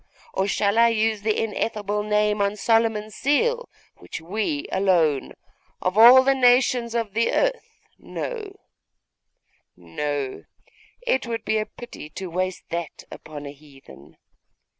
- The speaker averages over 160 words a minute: No, slow, 135 wpm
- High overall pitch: Yes, high, 210 Hz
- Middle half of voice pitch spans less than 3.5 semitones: No, average, 4.4 semitones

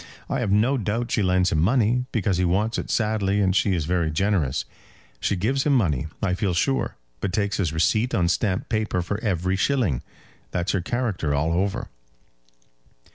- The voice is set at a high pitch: No, very low, 95 Hz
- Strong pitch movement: No, average, 3.7 semitones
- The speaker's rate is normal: Yes, average, 185 wpm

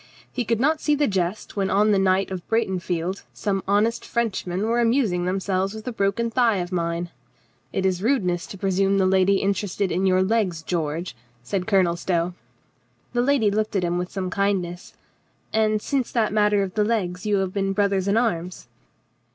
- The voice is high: Yes, high, 195 Hz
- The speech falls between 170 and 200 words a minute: Yes, average, 190 wpm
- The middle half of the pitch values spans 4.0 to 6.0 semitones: No, average, 3.0 semitones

